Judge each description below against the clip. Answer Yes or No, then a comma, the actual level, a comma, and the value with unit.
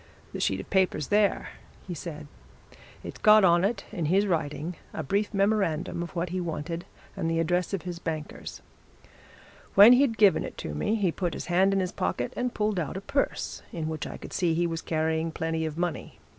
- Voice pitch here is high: No, medium, 175 Hz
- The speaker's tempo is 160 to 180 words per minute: No, fast, 205 wpm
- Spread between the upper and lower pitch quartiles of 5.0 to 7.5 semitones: No, average, 3.5 semitones